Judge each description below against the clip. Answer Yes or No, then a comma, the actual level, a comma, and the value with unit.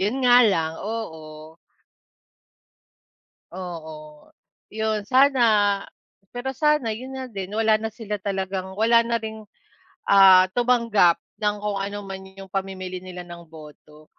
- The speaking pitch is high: Yes, high, 200 Hz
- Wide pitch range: No, average, 3.4 semitones